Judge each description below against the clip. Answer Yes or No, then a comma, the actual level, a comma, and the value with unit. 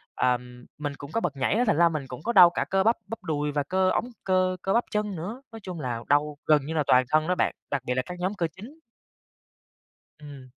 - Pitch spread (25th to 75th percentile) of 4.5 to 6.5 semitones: Yes, average, 5.2 semitones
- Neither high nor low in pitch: Yes, medium, 160 Hz